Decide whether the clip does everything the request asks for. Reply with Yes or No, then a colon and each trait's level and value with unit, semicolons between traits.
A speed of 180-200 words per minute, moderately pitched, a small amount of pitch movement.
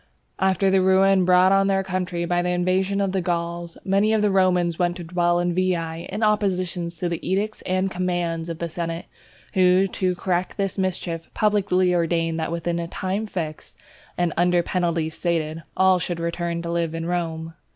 Yes: average, 185 wpm; medium, 180 Hz; narrow, 1.8 semitones